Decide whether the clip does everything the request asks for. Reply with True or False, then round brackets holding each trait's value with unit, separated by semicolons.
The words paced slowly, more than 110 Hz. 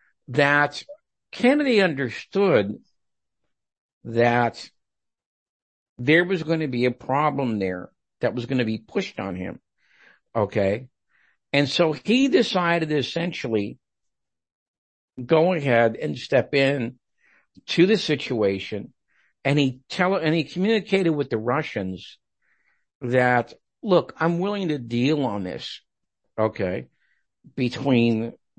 True (110 wpm; 135 Hz)